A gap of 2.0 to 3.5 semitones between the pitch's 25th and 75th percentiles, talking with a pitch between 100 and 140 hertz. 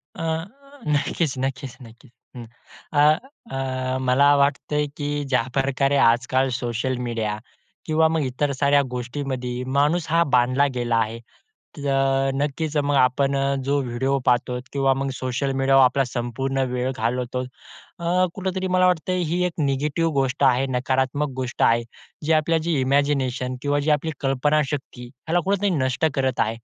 Yes: narrow, 2.5 semitones; low, 135 Hz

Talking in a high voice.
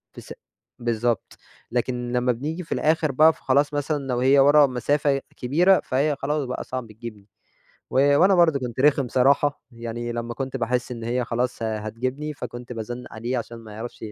No: low, 125 Hz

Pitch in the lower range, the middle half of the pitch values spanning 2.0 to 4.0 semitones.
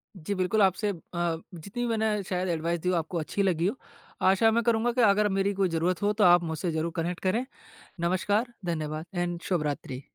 No: medium, 180 Hz; average, 3.5 semitones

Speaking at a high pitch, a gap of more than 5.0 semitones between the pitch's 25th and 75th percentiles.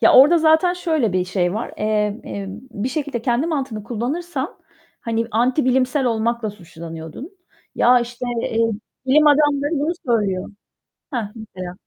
Yes: high, 240 Hz; wide, 5.4 semitones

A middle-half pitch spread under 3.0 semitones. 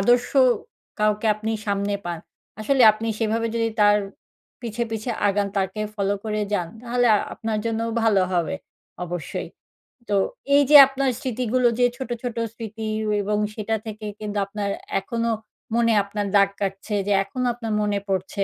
Yes: narrow, 2.5 semitones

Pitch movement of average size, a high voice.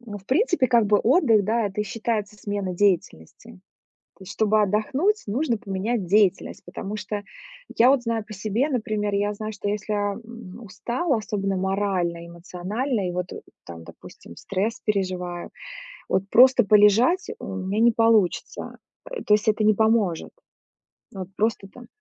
Yes: average, 3.1 semitones; high, 210 Hz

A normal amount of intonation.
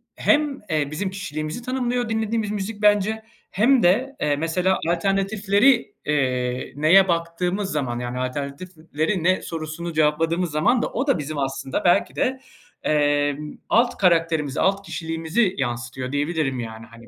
No: wide, 5.8 semitones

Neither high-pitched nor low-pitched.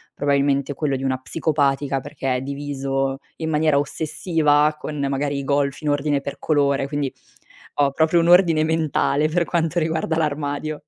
Yes: medium, 145 Hz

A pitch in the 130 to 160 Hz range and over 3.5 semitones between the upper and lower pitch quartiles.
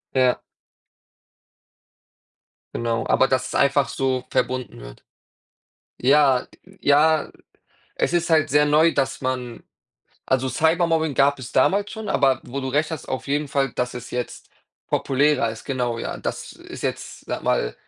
No: low, 135 Hz; average, 2.9 semitones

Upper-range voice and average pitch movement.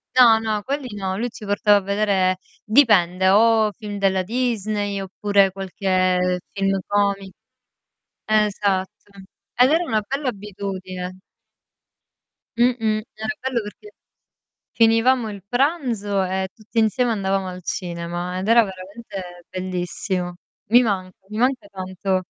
Yes: high, 205 Hz; average, 3.2 semitones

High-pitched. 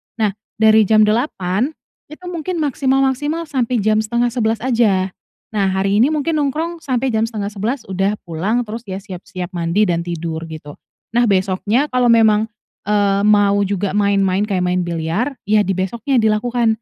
Yes: high, 215 Hz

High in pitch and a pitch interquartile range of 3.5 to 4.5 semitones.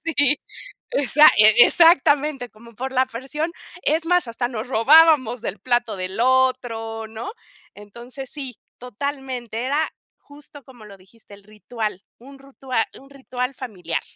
Yes: very high, 250 Hz; average, 3.8 semitones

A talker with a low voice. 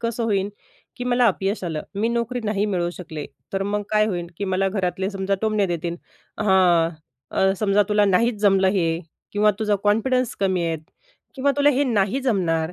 No: high, 200 Hz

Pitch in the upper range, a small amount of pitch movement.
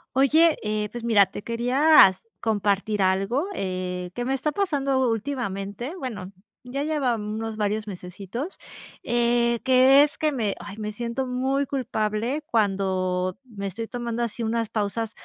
No: high, 230 Hz; average, 4.3 semitones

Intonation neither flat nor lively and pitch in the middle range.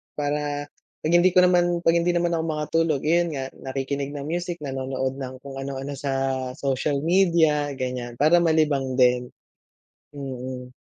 Yes: average, 3.8 semitones; medium, 145 Hz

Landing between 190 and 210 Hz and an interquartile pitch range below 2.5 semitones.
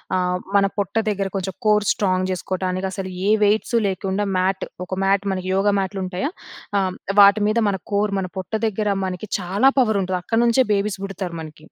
Yes: high, 195 Hz; narrow, 1.9 semitones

